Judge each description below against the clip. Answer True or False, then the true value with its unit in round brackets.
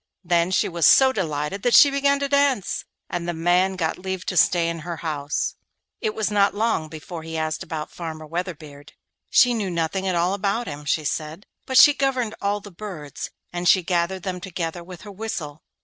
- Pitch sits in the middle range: True (180 Hz)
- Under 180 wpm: False (200 wpm)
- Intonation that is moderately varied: True (4.0 semitones)